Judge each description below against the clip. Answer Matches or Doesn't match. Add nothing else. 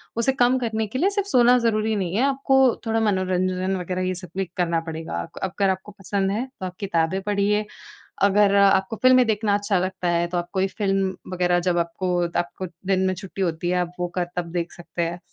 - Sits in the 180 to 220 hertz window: Matches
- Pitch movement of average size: Matches